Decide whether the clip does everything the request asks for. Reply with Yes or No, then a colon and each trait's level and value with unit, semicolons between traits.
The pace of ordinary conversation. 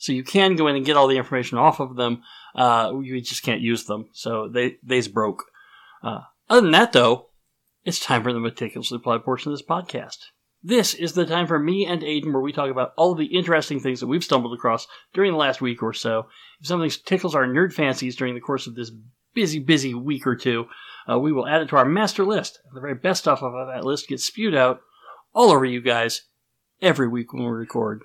No: fast, 235 wpm